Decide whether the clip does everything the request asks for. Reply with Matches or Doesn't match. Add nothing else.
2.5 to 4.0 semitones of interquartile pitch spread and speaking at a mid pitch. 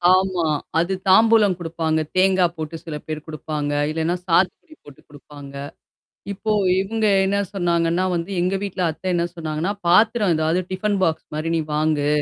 Matches